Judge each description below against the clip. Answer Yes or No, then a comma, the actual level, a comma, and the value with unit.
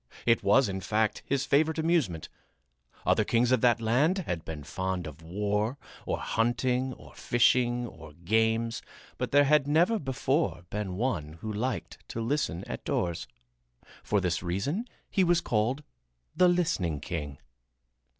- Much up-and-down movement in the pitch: Yes, wide, 6.9 semitones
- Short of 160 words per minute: Yes, average, 150 wpm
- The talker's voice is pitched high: No, low, 115 Hz